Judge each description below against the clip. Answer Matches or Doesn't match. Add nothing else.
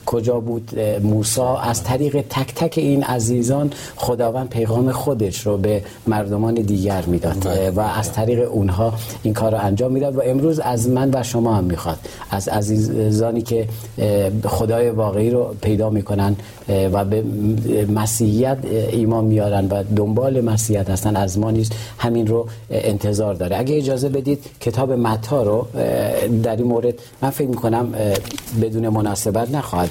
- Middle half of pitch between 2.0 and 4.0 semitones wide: Matches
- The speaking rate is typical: Matches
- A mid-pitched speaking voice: Doesn't match